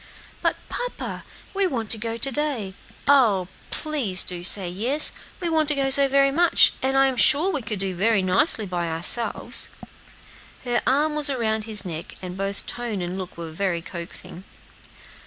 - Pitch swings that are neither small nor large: No, wide, 6.8 semitones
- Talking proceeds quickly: No, average, 175 wpm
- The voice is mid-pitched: No, high, 225 Hz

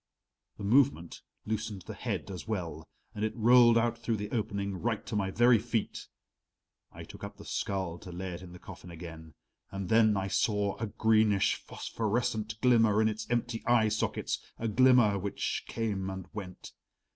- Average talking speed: Yes, average, 175 wpm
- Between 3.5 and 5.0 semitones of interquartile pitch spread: No, average, 3.1 semitones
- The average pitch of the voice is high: No, low, 105 Hz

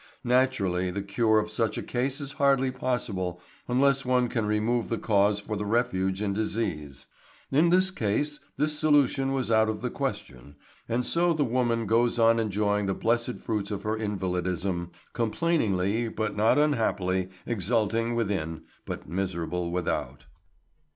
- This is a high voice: No, low, 110 Hz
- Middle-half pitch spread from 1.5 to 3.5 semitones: No, average, 4.2 semitones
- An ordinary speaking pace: Yes, average, 150 wpm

